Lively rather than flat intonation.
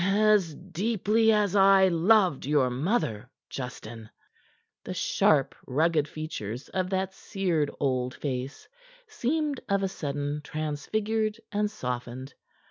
Yes: wide, 7.0 semitones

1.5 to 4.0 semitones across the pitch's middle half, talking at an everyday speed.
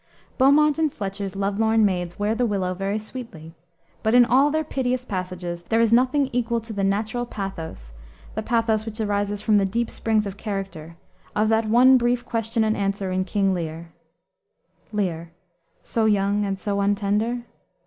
Yes: average, 3.0 semitones; average, 170 wpm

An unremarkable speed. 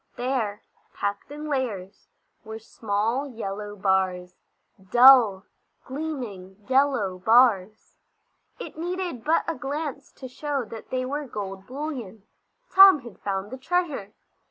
No: slow, 120 wpm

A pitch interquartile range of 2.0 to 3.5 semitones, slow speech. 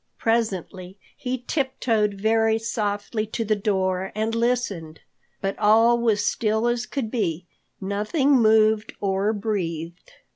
Yes: average, 2.8 semitones; slow, 115 wpm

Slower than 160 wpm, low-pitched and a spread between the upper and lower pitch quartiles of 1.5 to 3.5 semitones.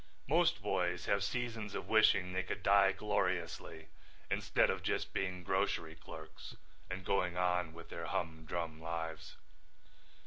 Yes: slow, 135 wpm; very low, 90 Hz; average, 2.9 semitones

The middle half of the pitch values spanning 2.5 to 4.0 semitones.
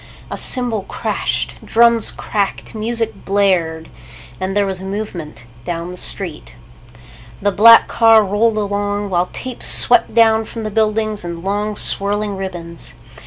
Yes: average, 2.8 semitones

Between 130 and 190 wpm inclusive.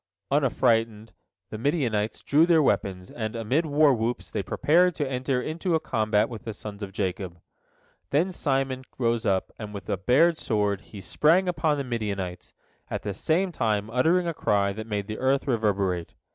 Yes: average, 170 wpm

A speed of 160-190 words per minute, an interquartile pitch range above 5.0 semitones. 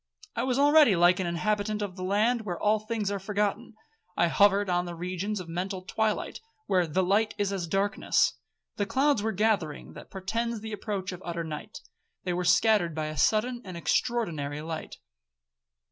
No: average, 175 wpm; average, 3.6 semitones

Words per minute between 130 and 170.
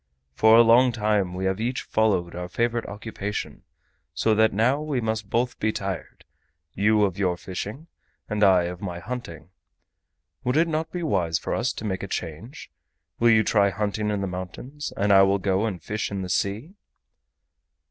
No: average, 185 wpm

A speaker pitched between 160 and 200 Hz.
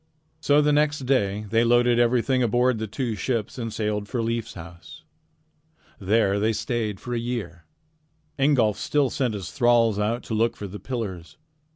No: low, 115 Hz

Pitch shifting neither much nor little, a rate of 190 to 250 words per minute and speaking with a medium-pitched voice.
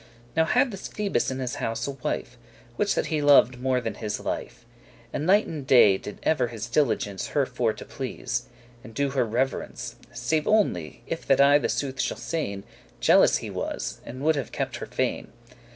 No: average, 4.1 semitones; average, 195 wpm; low, 130 Hz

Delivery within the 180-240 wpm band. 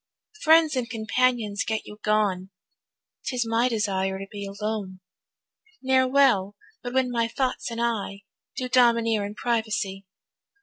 No: slow, 135 wpm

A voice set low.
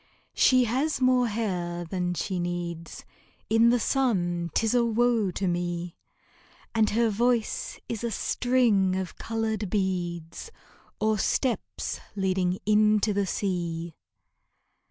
No: high, 205 Hz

